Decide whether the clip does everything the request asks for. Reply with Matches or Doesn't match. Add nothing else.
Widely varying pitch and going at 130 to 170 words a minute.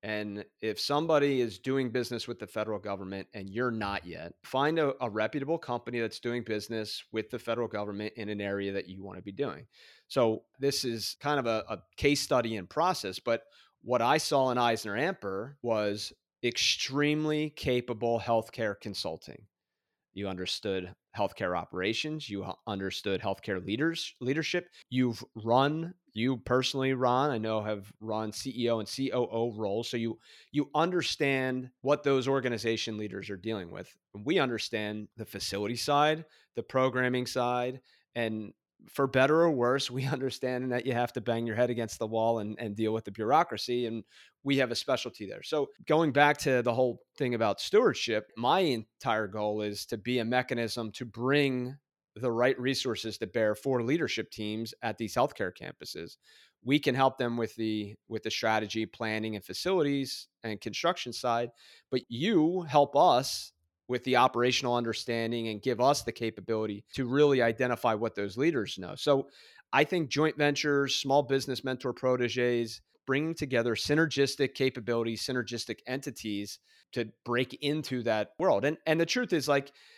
Doesn't match